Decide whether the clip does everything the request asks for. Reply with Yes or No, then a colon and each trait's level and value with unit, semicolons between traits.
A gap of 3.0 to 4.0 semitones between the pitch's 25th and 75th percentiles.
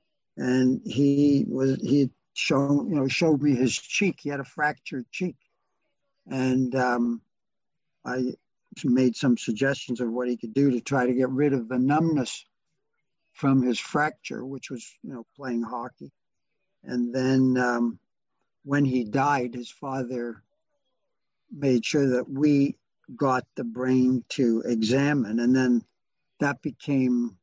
No: narrow, 2.5 semitones